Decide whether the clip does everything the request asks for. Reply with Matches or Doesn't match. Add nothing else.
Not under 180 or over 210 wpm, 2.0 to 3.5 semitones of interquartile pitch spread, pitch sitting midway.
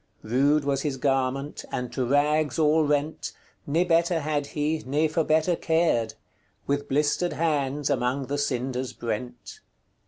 Doesn't match